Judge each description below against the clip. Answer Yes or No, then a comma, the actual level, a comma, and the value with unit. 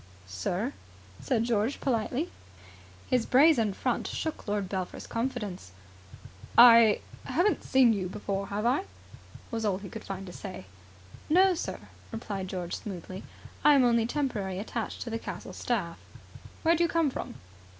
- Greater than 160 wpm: No, average, 150 wpm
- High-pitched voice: Yes, high, 225 Hz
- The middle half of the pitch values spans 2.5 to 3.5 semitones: No, average, 5.0 semitones